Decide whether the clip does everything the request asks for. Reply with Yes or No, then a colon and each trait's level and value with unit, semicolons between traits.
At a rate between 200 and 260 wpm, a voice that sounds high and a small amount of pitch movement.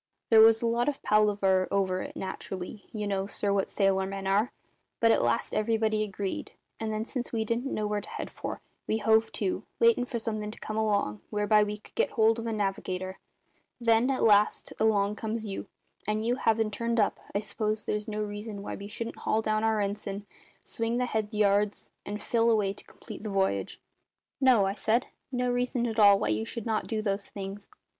Yes: fast, 205 wpm; high, 215 Hz; narrow, 2.0 semitones